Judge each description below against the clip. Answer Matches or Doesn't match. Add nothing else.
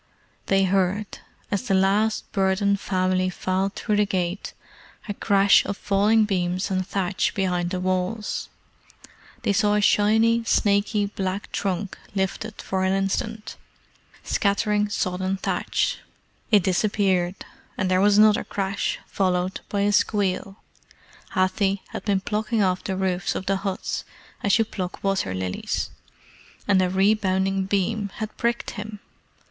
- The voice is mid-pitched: Doesn't match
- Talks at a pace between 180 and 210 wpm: Doesn't match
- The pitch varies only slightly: Matches